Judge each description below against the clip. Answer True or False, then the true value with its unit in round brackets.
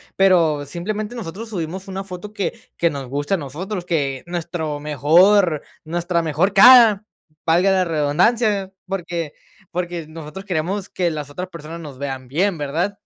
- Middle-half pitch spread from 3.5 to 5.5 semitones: True (4.1 semitones)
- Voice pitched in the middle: True (175 Hz)